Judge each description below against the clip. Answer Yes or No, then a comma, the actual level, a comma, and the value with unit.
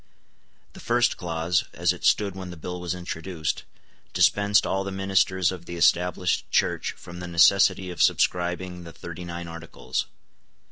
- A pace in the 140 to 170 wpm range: Yes, average, 155 wpm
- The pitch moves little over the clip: Yes, narrow, 1.5 semitones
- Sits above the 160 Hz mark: No, very low, 90 Hz